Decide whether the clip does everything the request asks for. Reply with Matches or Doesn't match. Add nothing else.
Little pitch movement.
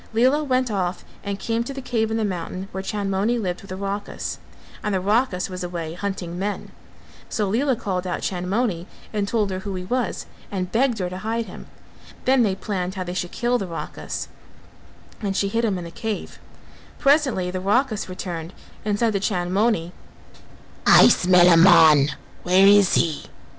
Doesn't match